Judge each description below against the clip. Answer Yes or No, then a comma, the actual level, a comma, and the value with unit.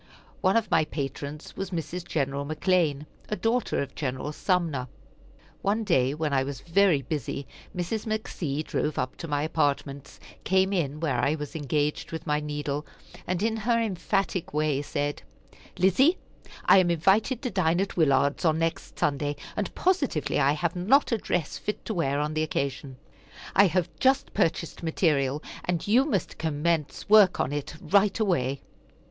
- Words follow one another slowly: No, average, 165 wpm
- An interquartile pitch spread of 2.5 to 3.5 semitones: No, average, 5.1 semitones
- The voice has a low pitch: No, medium, 160 Hz